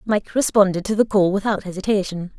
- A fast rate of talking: No, average, 175 wpm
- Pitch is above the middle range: Yes, high, 200 Hz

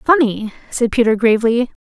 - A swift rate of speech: No, slow, 130 wpm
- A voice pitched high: Yes, high, 235 Hz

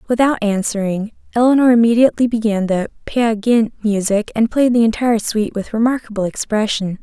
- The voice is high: Yes, high, 220 Hz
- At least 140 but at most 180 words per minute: Yes, average, 145 wpm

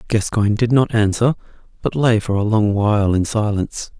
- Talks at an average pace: Yes, average, 180 wpm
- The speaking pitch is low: Yes, low, 110 Hz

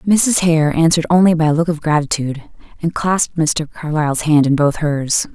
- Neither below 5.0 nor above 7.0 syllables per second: Yes, 5.4 syllables/s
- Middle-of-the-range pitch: Yes, medium, 160 Hz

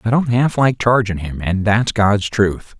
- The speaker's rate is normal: No, fast, 215 wpm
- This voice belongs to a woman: No, male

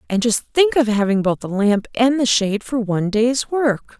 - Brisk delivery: Yes, fast, 225 wpm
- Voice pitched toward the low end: No, high, 230 Hz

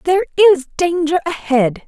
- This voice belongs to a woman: Yes, female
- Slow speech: Yes, slow, 130 wpm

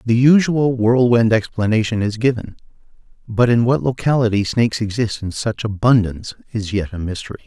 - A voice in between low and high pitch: No, low, 115 Hz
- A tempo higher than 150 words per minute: No, average, 145 wpm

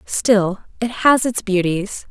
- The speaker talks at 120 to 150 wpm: Yes, average, 140 wpm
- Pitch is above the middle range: Yes, high, 210 Hz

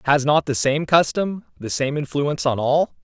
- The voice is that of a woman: No, male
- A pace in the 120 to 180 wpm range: No, average, 200 wpm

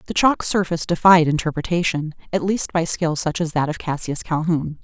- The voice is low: No, medium, 165 Hz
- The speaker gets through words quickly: No, average, 175 wpm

